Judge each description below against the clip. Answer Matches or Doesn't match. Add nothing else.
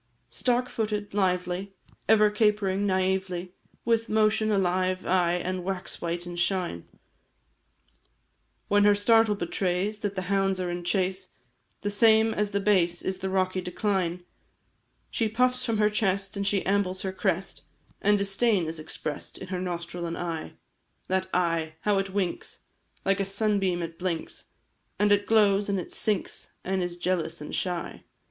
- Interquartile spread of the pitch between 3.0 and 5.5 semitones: Doesn't match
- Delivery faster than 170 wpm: Doesn't match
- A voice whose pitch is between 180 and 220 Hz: Matches